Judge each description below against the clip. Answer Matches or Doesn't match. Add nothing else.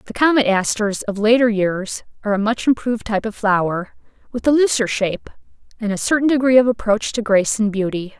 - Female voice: Matches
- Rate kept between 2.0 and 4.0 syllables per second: Doesn't match